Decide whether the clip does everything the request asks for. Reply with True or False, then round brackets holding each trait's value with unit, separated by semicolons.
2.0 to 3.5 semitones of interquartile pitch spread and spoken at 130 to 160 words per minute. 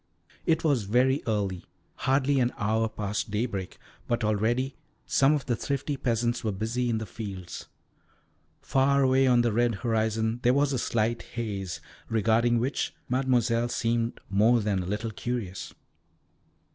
True (2.9 semitones; 145 wpm)